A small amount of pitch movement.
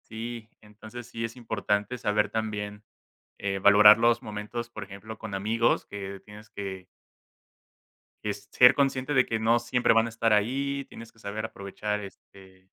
Yes: narrow, 2.2 semitones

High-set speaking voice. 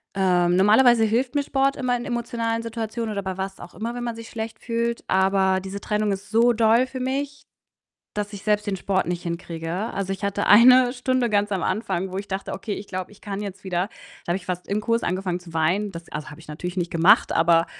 Yes: high, 205 Hz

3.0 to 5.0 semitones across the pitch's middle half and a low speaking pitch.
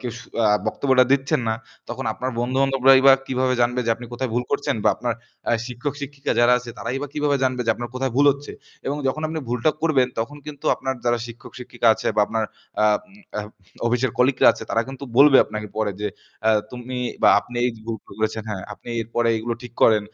No: narrow, 2.4 semitones; low, 125 Hz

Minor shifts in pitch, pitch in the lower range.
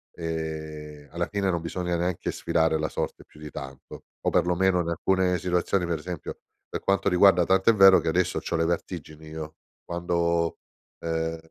Yes: narrow, 2.2 semitones; very low, 85 Hz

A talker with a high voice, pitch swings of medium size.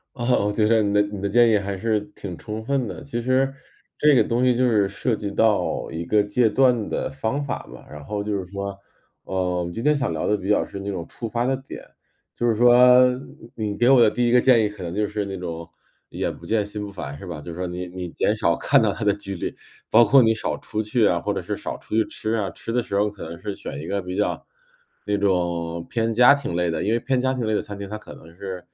No: low, 105 Hz; average, 3.7 semitones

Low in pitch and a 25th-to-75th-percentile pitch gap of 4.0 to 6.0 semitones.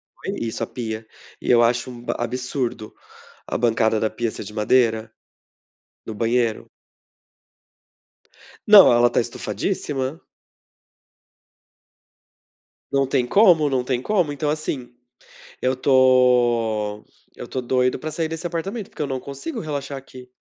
No: low, 125 Hz; average, 3.6 semitones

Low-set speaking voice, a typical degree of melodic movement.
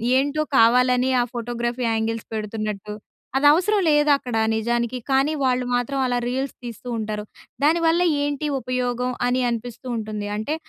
No: very high, 250 Hz; average, 3.2 semitones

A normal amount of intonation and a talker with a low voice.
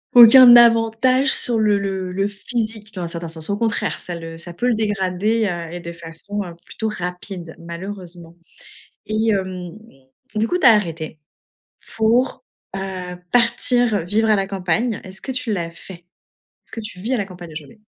No: average, 4.2 semitones; high, 195 Hz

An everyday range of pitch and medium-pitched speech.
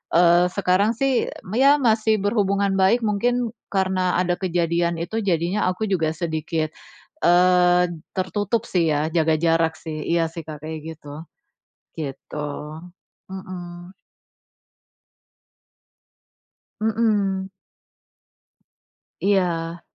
Yes: average, 3.5 semitones; medium, 180 Hz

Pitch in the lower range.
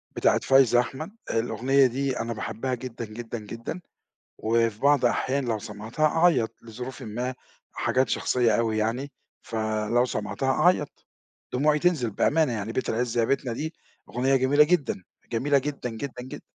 Yes: low, 125 Hz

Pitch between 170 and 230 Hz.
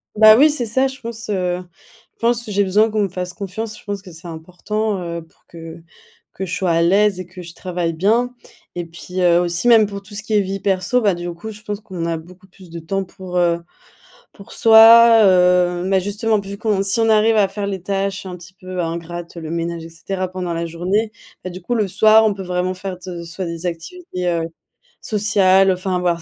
Yes: high, 190 Hz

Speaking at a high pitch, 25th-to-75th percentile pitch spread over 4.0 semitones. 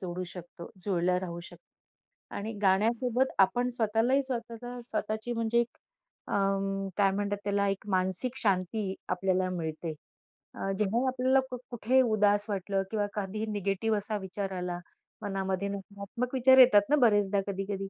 No: high, 205 Hz; average, 3.3 semitones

